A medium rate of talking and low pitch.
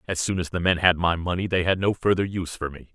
No: fast, 305 wpm; very low, 90 Hz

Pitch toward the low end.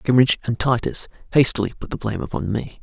Yes: low, 125 Hz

